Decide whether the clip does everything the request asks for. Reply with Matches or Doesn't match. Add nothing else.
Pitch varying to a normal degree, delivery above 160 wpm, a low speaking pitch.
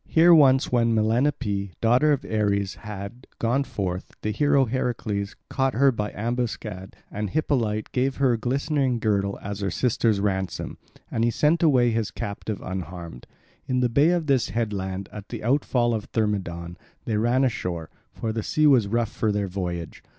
Matches